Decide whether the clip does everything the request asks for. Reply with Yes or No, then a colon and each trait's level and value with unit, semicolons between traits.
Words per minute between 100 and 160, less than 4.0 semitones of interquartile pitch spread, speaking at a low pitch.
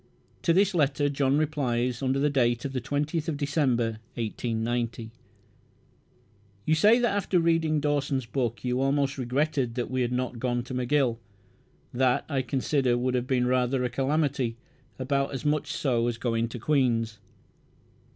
Yes: average, 145 wpm; average, 3.1 semitones; low, 130 Hz